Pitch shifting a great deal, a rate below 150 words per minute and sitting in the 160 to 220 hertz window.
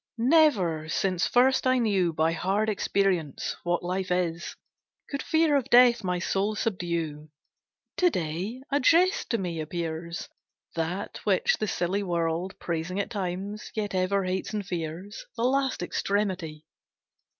No: average, 4.4 semitones; average, 140 wpm; high, 190 Hz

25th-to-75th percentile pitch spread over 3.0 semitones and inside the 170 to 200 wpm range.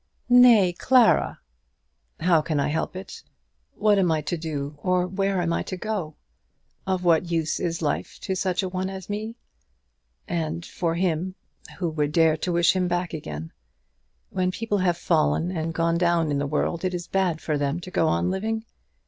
No: average, 2.7 semitones; average, 185 wpm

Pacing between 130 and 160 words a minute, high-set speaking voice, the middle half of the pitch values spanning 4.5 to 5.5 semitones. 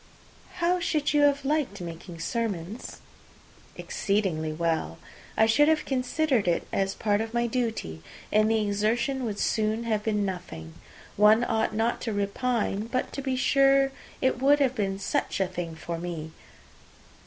Yes: average, 155 wpm; high, 220 Hz; average, 5.0 semitones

